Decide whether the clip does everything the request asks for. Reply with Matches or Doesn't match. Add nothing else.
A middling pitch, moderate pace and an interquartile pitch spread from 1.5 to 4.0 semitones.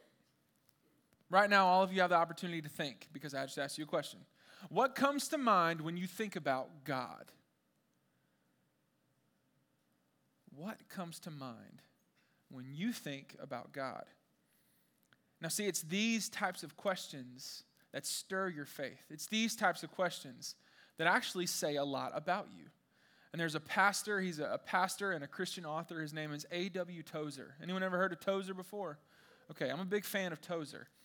Doesn't match